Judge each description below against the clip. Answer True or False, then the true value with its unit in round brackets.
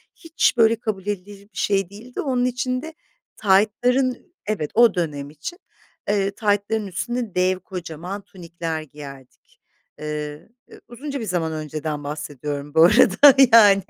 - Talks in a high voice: True (195 Hz)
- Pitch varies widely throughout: True (6.4 semitones)